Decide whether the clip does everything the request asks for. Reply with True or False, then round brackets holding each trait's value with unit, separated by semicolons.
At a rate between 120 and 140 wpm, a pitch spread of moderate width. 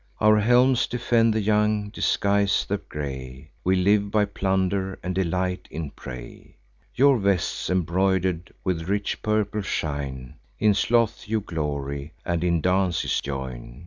True (135 wpm; 4.8 semitones)